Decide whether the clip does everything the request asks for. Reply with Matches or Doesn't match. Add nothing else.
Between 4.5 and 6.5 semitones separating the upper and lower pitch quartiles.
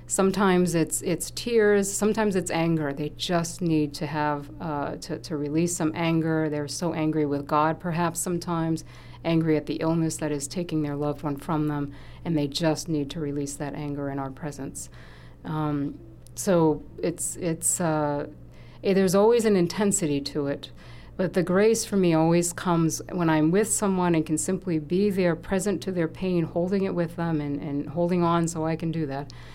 Doesn't match